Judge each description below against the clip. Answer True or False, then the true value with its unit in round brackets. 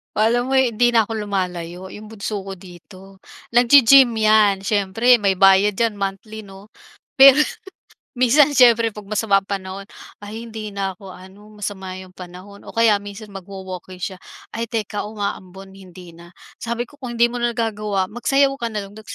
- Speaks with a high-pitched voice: True (205 Hz)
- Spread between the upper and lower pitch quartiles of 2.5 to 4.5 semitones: True (3.1 semitones)